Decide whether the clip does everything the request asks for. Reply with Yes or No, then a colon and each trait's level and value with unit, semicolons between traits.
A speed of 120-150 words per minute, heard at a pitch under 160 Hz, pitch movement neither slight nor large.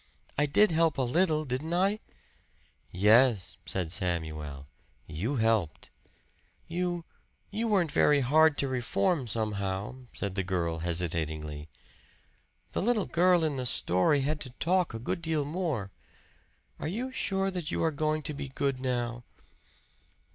No: average, 140 wpm; low, 135 Hz; wide, 8.8 semitones